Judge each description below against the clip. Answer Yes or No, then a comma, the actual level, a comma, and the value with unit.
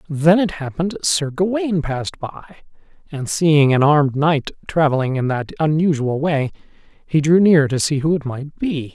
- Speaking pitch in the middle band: Yes, medium, 150 Hz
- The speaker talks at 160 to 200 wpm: Yes, average, 175 wpm